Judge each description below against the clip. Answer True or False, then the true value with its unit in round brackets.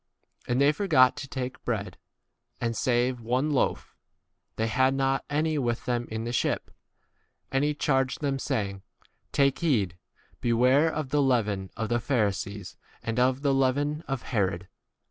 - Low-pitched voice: True (130 Hz)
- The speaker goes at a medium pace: True (165 wpm)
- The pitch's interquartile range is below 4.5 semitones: True (3.3 semitones)